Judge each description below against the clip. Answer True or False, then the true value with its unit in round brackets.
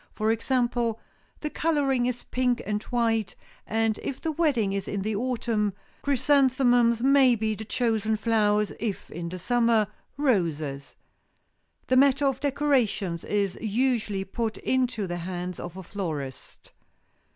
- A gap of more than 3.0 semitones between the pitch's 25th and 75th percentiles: True (4.2 semitones)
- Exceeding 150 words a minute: False (140 wpm)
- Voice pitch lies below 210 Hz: False (225 Hz)